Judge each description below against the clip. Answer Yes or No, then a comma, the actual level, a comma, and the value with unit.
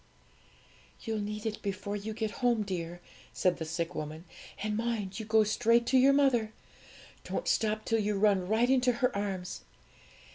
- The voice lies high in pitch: Yes, high, 215 Hz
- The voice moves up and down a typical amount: Yes, average, 3.0 semitones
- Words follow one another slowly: No, average, 170 wpm